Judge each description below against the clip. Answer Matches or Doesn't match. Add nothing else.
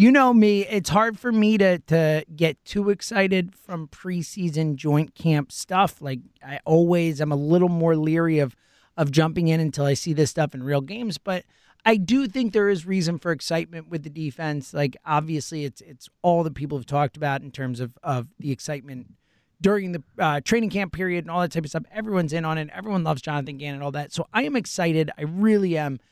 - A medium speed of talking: Doesn't match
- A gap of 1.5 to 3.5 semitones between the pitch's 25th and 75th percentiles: Doesn't match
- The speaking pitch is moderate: Matches